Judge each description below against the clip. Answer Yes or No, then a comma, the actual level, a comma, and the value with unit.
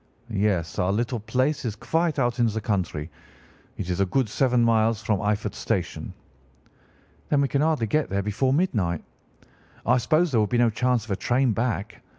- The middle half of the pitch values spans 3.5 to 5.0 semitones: Yes, average, 4.2 semitones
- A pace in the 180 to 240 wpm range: Yes, average, 185 wpm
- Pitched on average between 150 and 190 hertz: No, low, 115 Hz